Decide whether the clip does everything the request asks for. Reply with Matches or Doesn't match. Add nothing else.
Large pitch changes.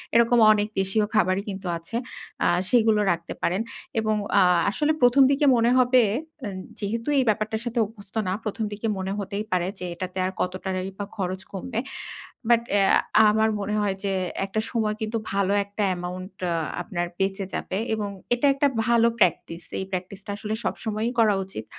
Doesn't match